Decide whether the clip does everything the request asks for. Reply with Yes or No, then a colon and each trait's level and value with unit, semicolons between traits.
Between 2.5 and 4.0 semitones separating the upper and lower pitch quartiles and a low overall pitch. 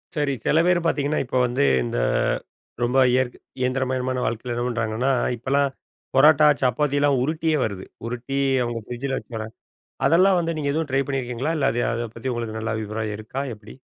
Yes: average, 3.3 semitones; low, 130 Hz